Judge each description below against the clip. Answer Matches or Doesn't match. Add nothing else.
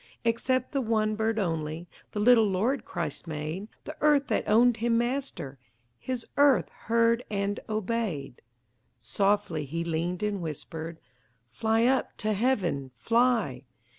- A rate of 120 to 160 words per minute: Matches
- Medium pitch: Doesn't match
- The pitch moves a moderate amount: Doesn't match